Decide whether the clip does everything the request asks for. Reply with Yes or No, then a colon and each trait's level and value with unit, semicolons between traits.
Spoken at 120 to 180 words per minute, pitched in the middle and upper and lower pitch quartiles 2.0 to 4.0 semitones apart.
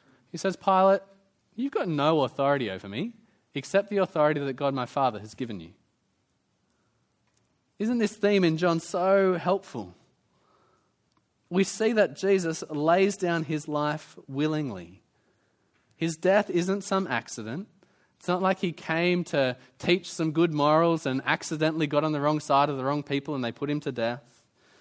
No: average, 160 wpm; medium, 160 Hz; average, 5.2 semitones